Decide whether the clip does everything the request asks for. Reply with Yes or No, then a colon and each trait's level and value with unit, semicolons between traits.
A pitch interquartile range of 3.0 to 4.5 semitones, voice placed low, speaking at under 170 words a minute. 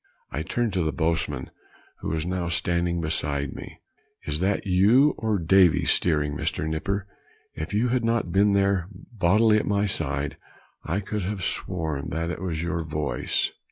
Yes: average, 4.2 semitones; very low, 90 Hz; average, 160 wpm